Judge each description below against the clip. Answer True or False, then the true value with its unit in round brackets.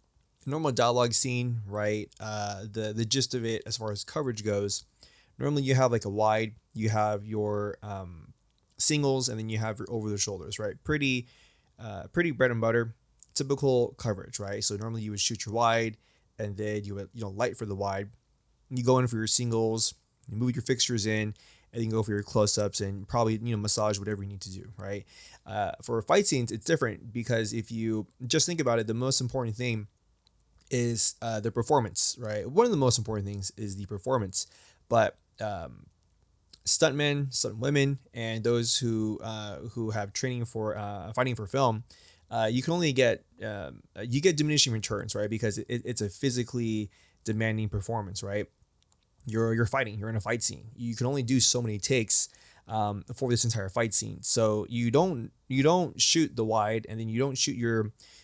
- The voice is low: True (110 Hz)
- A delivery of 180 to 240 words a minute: True (195 wpm)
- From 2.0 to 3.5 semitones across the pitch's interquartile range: True (2.9 semitones)